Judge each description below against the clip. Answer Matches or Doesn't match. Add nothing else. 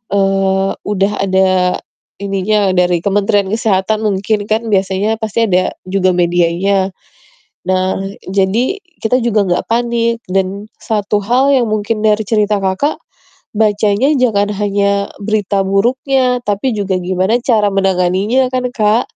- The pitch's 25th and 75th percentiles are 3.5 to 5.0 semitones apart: Doesn't match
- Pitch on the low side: Doesn't match